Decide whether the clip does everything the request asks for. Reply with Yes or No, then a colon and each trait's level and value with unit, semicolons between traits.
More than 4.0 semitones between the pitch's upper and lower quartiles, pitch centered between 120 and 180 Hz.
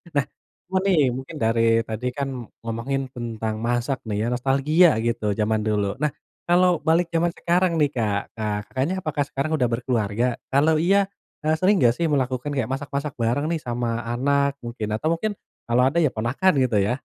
Yes: average, 4.9 semitones; low, 135 Hz